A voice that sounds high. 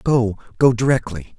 No: low, 115 Hz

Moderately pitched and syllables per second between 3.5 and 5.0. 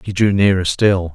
No: very low, 95 Hz; 4.8 syllables/s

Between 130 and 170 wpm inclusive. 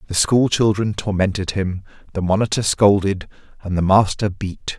Yes: average, 150 wpm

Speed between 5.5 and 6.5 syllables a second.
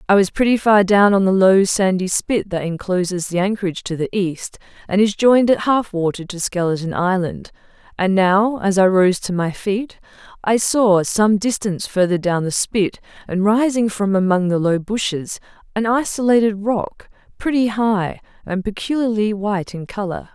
No: 4.8 syllables/s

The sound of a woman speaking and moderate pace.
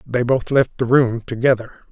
No: male; average, 190 wpm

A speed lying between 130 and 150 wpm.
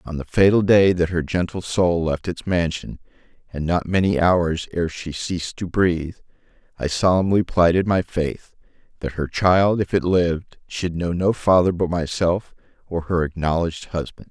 No: average, 170 wpm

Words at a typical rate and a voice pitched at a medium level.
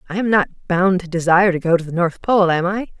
No: fast, 280 wpm; medium, 180 Hz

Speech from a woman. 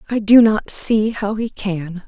Yes: female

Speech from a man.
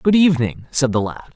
Yes: male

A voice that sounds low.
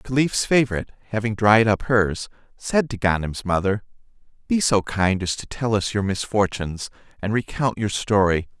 Yes: low, 105 Hz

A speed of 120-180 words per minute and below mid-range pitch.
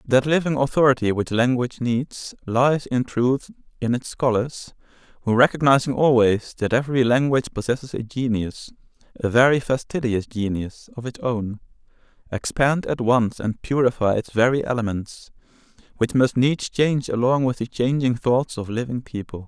Yes: average, 150 wpm; low, 125 Hz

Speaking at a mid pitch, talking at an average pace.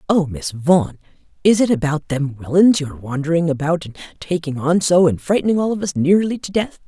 No: medium, 165 Hz; fast, 210 wpm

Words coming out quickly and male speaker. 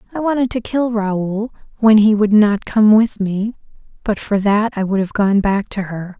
No: fast, 215 wpm; female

